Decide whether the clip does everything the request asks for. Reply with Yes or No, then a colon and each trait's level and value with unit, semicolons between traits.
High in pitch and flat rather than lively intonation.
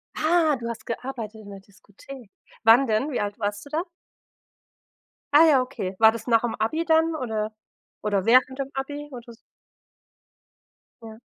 No: high, 235 Hz; average, 4.1 semitones